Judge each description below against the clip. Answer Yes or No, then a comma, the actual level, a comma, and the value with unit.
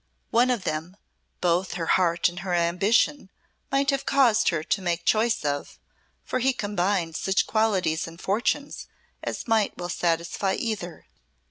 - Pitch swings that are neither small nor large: Yes, average, 4.8 semitones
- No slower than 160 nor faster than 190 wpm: No, average, 150 wpm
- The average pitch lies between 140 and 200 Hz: Yes, high, 190 Hz